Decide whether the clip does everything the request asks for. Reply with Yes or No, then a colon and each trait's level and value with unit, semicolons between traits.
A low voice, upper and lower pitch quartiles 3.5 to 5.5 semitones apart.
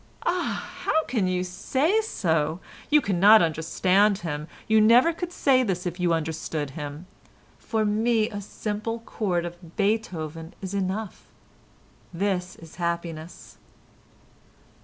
No: high, 190 Hz; average, 4.7 semitones